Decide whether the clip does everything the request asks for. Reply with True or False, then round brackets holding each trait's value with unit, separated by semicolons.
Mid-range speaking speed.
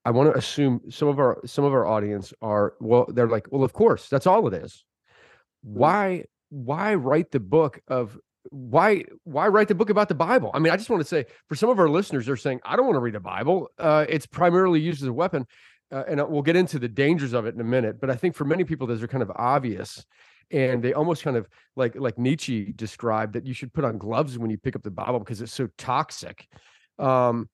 False (250 wpm)